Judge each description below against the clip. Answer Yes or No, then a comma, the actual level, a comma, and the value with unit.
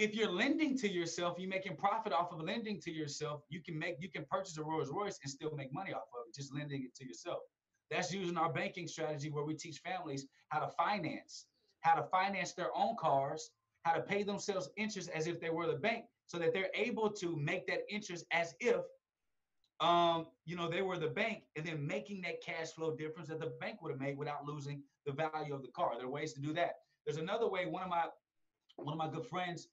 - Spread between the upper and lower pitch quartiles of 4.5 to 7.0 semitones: No, average, 3.5 semitones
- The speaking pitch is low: No, medium, 165 Hz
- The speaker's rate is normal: No, fast, 235 wpm